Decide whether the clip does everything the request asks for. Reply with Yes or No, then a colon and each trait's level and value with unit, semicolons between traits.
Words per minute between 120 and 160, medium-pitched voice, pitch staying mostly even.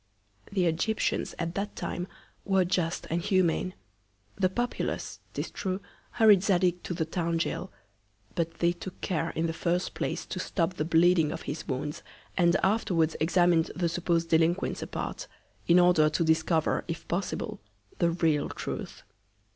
Yes: average, 155 wpm; medium, 170 Hz; narrow, 2.0 semitones